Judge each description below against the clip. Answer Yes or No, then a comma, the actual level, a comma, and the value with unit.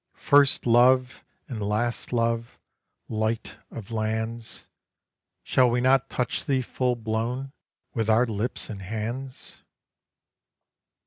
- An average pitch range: No, narrow, 2.3 semitones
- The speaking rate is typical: No, slow, 110 wpm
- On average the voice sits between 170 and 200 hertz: No, low, 115 Hz